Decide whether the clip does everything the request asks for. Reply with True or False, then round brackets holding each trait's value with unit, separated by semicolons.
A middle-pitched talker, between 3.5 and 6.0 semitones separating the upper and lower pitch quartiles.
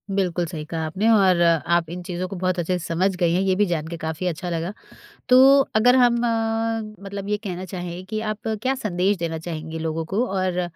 False (180 Hz; 2.8 semitones)